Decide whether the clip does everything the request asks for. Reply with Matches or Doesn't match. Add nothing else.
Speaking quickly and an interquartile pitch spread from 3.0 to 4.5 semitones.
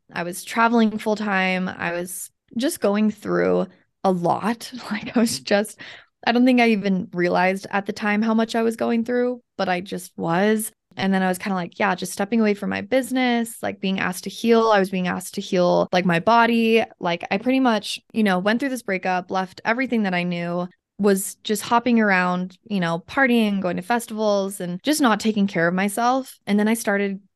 Matches